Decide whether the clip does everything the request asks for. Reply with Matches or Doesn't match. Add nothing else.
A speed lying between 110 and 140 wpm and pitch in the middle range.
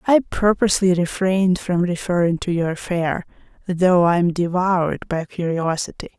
Matches